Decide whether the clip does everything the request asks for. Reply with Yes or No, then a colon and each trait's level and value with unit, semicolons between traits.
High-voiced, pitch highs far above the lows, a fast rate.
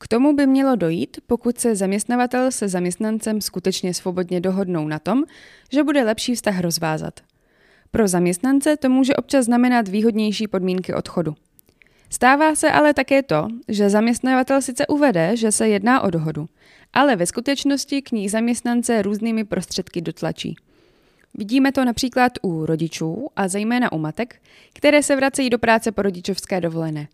No: high, 225 Hz; wide, 5.8 semitones; average, 155 wpm